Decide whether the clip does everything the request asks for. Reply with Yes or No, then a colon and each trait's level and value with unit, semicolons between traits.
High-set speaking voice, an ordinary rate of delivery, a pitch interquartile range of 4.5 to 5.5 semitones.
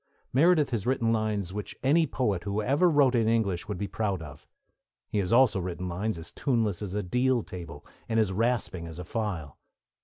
No: low, 105 Hz; average, 195 wpm; average, 5.1 semitones